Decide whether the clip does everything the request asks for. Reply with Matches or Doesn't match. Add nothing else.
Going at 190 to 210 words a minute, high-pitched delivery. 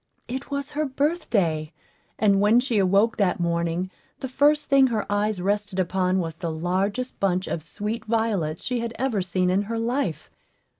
Doesn't match